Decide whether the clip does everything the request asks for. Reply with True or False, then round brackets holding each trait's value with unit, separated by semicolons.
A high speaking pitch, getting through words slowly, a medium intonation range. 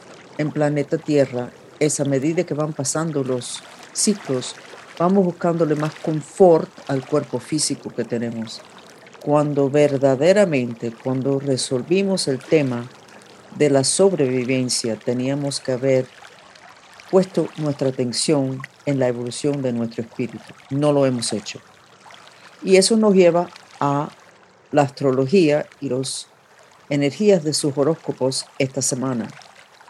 False (140 Hz; 120 wpm; 3.4 semitones)